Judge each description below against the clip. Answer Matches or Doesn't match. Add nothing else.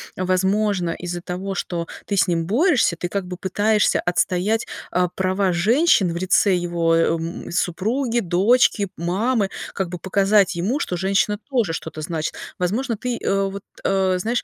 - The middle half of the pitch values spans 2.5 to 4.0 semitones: Matches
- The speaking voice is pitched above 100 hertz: Matches